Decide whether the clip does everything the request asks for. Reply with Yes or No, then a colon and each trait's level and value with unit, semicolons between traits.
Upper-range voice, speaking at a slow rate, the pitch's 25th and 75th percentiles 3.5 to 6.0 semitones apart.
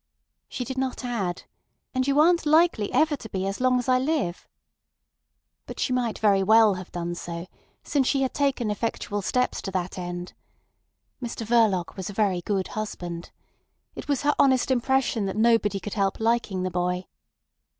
No: high, 220 Hz; average, 175 wpm; average, 5.3 semitones